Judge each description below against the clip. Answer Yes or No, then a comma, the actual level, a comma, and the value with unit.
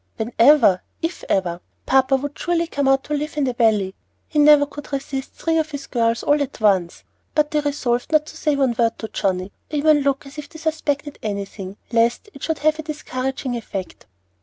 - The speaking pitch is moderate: No, very high, 275 Hz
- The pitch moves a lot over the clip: No, average, 4.5 semitones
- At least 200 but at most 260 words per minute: Yes, fast, 205 wpm